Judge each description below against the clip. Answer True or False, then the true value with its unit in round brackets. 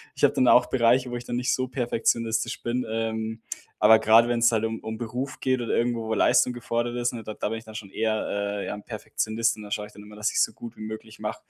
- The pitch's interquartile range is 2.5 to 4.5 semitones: False (1.7 semitones)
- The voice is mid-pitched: False (115 Hz)